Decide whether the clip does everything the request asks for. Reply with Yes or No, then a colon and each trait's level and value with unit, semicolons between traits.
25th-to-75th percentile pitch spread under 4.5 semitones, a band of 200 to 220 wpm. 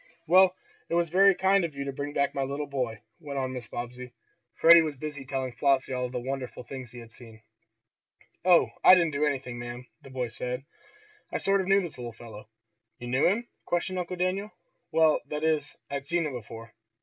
No: average, 5.2 semitones; fast, 205 wpm